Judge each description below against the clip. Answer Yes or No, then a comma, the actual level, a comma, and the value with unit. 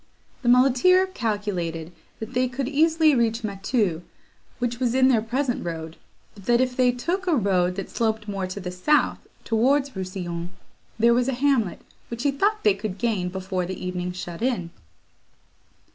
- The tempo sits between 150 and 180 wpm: Yes, average, 170 wpm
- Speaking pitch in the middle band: No, high, 230 Hz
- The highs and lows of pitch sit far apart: Yes, wide, 5.8 semitones